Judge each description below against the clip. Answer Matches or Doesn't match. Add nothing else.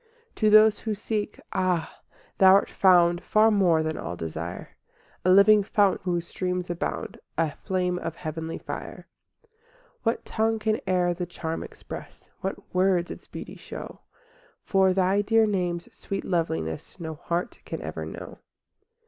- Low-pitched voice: Doesn't match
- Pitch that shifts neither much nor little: Matches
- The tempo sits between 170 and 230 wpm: Doesn't match